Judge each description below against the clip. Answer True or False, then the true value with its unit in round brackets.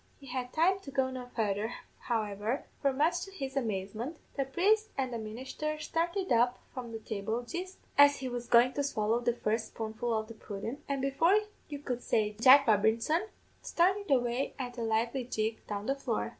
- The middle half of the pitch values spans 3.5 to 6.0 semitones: True (4.2 semitones)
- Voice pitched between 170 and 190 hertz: False (250 Hz)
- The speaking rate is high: False (190 wpm)